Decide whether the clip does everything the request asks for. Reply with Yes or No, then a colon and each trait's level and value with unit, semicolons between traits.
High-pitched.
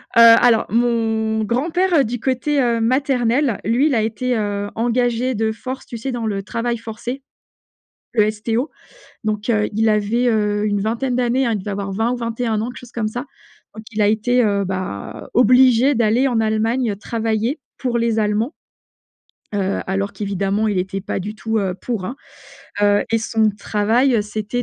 Yes: high, 225 Hz